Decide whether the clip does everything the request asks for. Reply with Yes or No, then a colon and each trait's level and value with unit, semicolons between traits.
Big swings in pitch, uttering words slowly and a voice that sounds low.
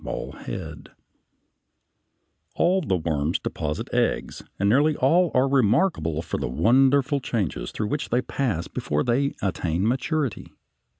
Yes: wide, 8.7 semitones; slow, 125 wpm; low, 120 Hz